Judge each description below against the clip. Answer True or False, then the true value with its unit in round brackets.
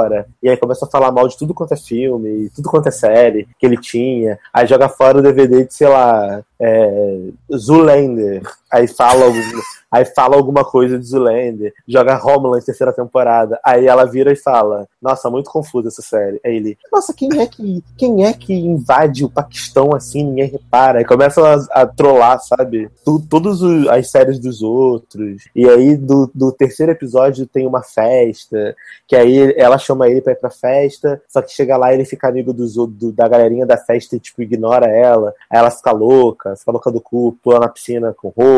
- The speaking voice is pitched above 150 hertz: False (130 Hz)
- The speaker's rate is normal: False (200 wpm)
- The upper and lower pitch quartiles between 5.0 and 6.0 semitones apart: False (2.9 semitones)